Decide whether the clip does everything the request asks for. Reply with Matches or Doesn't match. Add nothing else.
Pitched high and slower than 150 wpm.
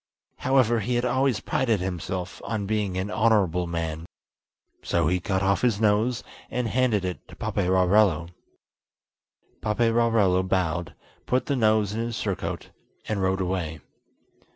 Doesn't match